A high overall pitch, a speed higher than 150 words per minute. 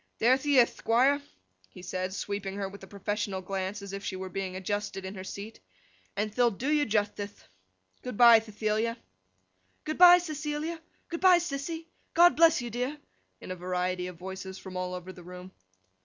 Yes: high, 205 Hz; average, 180 wpm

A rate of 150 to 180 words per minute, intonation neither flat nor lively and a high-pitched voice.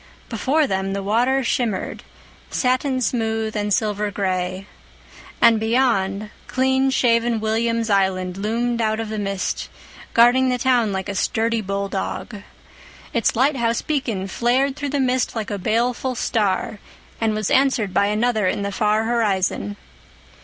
No: average, 140 wpm; average, 3.5 semitones; high, 225 Hz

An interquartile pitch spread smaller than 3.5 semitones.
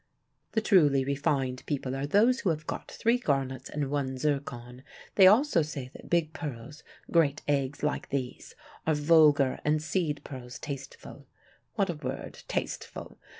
Yes: average, 3.1 semitones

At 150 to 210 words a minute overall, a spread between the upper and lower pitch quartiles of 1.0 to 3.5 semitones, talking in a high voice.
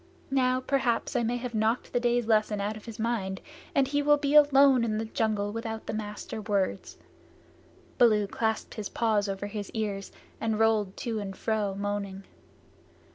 Yes: average, 175 wpm; average, 2.8 semitones; high, 220 Hz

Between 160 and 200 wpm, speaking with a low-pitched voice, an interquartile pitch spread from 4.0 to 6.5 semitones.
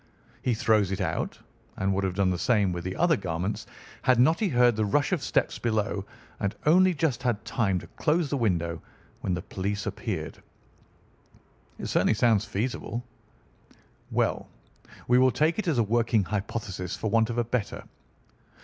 Yes: average, 175 wpm; low, 110 Hz; average, 4.5 semitones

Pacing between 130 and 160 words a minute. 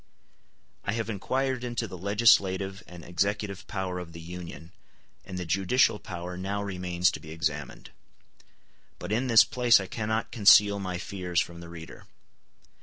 Yes: average, 155 wpm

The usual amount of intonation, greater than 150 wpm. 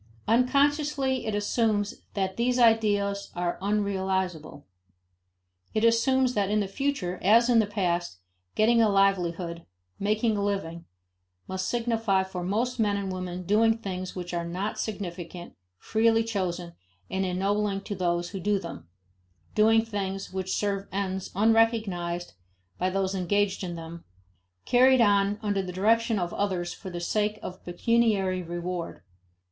No: average, 3.5 semitones; average, 140 wpm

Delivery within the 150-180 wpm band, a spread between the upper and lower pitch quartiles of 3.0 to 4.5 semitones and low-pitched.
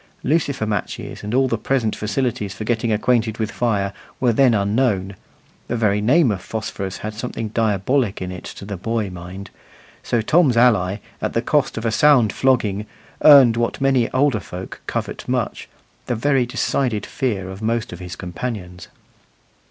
Yes: average, 170 wpm; average, 3.9 semitones; low, 110 Hz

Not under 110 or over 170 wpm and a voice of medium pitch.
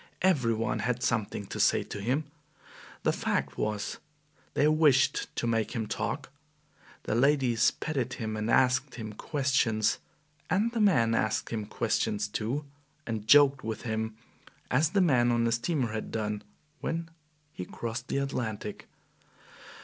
No: average, 150 wpm; low, 120 Hz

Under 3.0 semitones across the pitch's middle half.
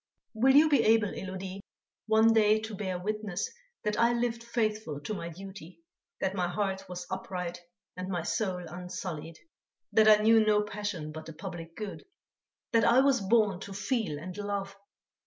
No: average, 3.3 semitones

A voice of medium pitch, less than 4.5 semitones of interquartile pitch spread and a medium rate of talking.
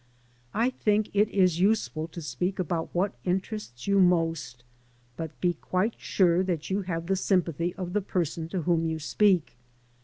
Yes: medium, 180 Hz; average, 2.9 semitones; average, 165 wpm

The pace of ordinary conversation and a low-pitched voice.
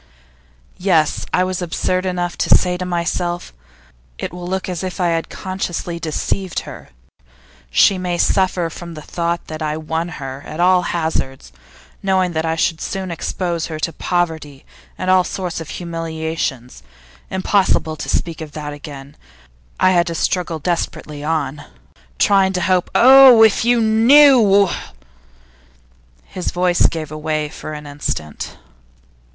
No: average, 150 wpm; medium, 170 Hz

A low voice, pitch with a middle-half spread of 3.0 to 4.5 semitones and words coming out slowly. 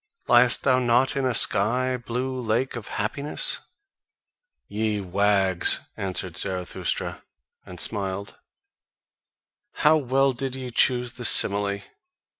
Yes: low, 120 Hz; average, 4.2 semitones; slow, 110 wpm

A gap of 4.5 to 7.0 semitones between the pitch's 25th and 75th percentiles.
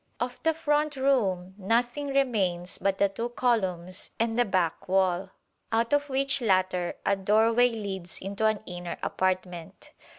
Yes: average, 4.8 semitones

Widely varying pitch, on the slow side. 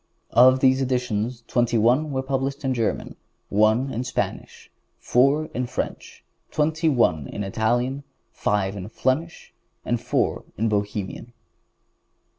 No: average, 3.5 semitones; slow, 125 wpm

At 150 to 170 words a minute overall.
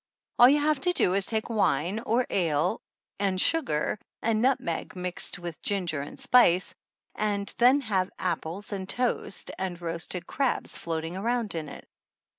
Yes: average, 155 wpm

